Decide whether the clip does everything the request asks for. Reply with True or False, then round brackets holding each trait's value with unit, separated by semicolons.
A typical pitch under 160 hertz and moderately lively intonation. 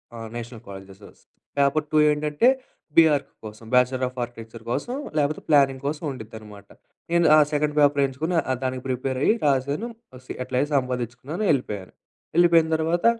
True (135 Hz; 3.9 semitones)